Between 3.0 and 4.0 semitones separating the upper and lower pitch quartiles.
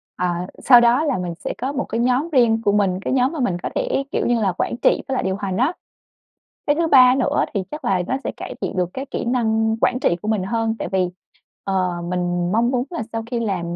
No: average, 5.2 semitones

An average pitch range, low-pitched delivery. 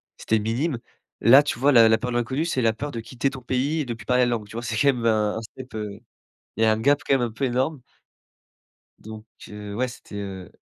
Yes: average, 3.1 semitones; low, 120 Hz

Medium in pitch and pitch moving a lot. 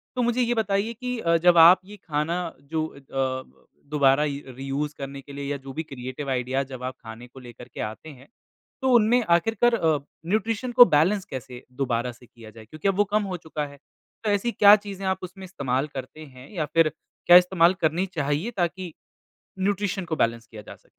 Yes: medium, 160 Hz; wide, 6.4 semitones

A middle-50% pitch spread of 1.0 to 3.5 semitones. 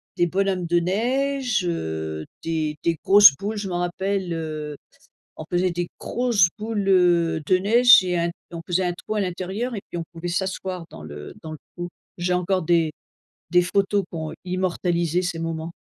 Yes: average, 2.8 semitones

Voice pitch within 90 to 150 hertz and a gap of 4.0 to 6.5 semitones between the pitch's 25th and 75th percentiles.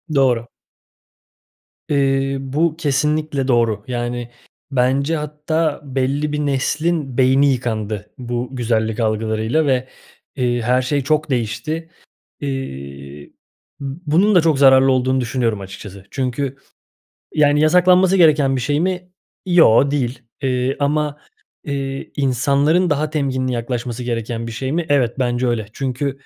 No: low, 135 Hz; average, 3.5 semitones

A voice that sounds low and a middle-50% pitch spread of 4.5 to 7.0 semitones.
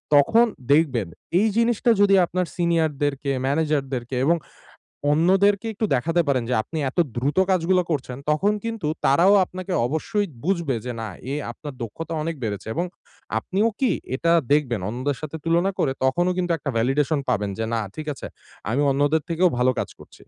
No: medium, 155 Hz; average, 5.2 semitones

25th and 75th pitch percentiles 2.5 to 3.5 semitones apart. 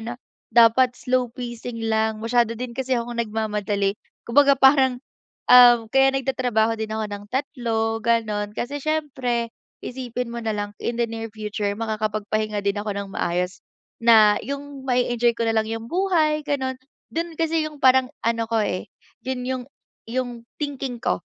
Yes: average, 3.0 semitones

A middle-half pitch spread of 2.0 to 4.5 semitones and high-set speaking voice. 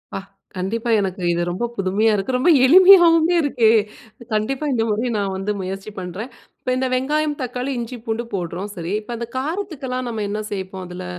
No: average, 5.3 semitones; high, 225 Hz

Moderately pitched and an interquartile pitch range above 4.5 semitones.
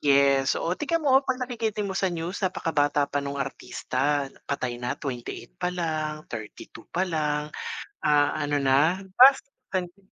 Yes: medium, 155 Hz; average, 5.1 semitones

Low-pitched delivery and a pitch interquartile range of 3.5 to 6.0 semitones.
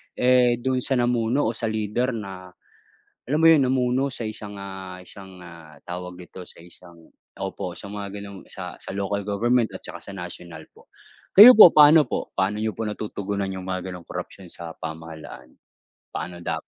Yes: low, 100 Hz; average, 5.1 semitones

